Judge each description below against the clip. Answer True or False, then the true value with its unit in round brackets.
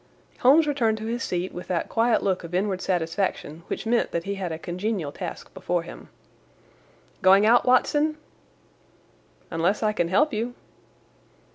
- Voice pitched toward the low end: False (195 Hz)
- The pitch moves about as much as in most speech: True (4.8 semitones)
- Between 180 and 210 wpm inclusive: False (155 wpm)